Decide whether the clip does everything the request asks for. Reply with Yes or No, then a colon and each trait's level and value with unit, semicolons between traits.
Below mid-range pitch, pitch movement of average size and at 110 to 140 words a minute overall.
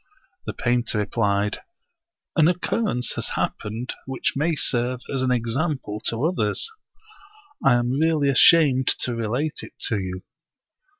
Yes: low, 125 Hz; average, 4.7 semitones; slow, 135 wpm